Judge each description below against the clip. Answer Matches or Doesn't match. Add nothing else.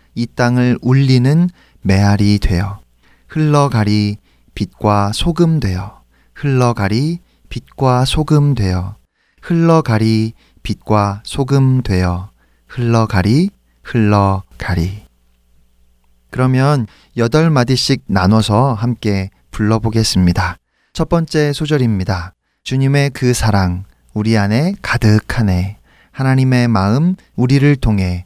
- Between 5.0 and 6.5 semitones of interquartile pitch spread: Matches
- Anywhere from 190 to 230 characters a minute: Matches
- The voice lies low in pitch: Matches